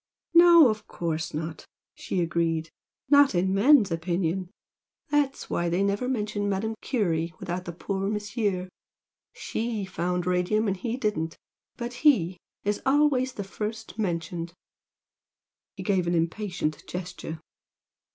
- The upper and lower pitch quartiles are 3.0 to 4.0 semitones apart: No, average, 4.5 semitones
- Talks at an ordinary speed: No, slow, 125 wpm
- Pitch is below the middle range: No, high, 195 Hz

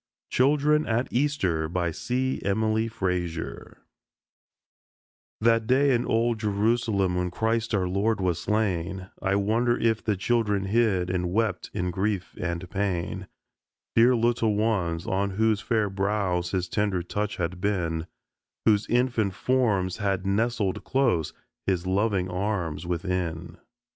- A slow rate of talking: Yes, slow, 130 wpm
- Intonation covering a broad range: No, average, 3.8 semitones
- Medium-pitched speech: No, low, 100 Hz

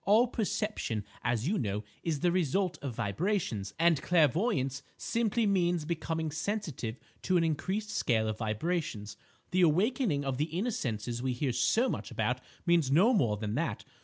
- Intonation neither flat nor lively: No, wide, 7.8 semitones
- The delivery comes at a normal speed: Yes, average, 165 wpm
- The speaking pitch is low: No, medium, 160 Hz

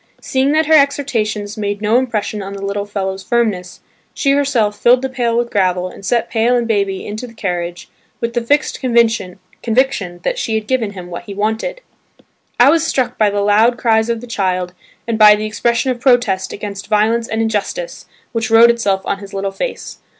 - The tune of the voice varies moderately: Yes, average, 3.3 semitones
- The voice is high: Yes, high, 220 Hz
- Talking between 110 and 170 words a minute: No, average, 195 wpm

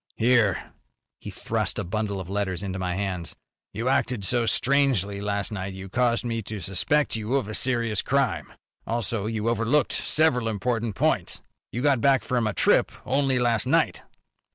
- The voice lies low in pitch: Yes, low, 115 Hz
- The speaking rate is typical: Yes, average, 170 wpm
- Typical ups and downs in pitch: Yes, average, 3.8 semitones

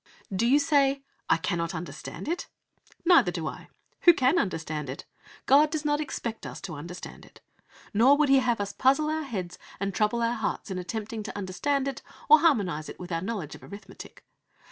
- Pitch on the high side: Yes, high, 225 Hz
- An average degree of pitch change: No, wide, 7.7 semitones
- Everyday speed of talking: Yes, average, 190 wpm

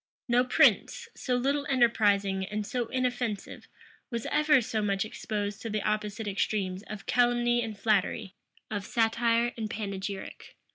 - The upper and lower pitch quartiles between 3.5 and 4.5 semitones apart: No, average, 3.0 semitones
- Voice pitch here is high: Yes, high, 220 Hz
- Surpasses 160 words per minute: No, average, 140 wpm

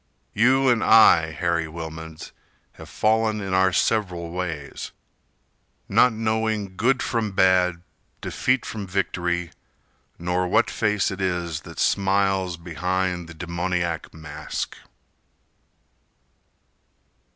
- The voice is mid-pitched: No, very low, 90 Hz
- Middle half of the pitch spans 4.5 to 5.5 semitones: No, average, 3.7 semitones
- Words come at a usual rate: No, slow, 105 wpm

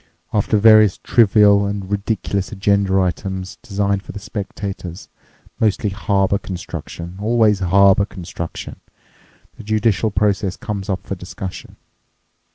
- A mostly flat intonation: Yes, narrow, 1.6 semitones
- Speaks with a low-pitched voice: Yes, low, 100 Hz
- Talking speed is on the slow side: Yes, slow, 100 wpm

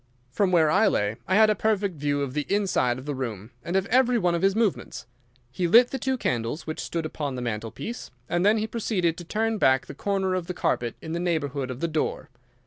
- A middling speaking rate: No, fast, 235 wpm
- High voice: No, medium, 170 Hz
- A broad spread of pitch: Yes, wide, 6.6 semitones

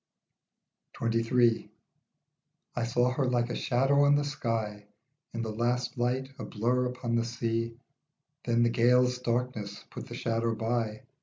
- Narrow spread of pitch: Yes, narrow, 1.5 semitones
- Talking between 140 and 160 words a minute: Yes, average, 150 wpm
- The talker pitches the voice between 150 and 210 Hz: No, low, 120 Hz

